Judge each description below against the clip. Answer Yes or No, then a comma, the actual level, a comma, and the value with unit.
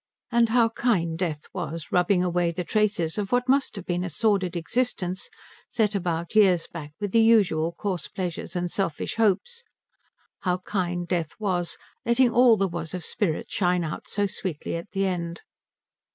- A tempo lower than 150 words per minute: No, average, 170 wpm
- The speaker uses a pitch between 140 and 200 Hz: Yes, medium, 185 Hz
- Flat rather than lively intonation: No, average, 3.8 semitones